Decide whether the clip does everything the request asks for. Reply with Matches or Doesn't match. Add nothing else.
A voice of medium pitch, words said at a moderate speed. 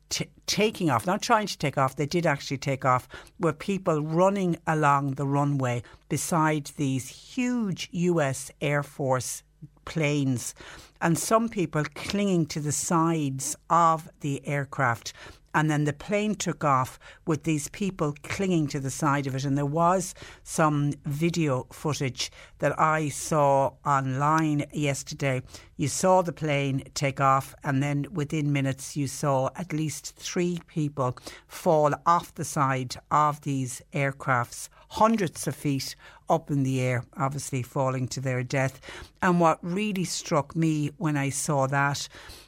Matches